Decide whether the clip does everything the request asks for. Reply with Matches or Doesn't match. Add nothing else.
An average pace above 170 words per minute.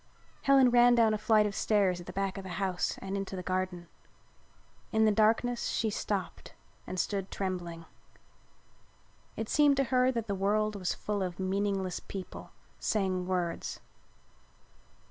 Doesn't match